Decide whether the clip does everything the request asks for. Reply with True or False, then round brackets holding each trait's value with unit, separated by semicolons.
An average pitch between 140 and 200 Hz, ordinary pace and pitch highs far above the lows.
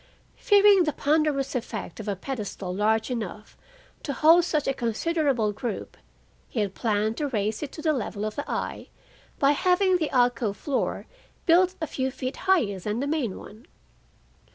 False (260 Hz; 170 wpm; 6.3 semitones)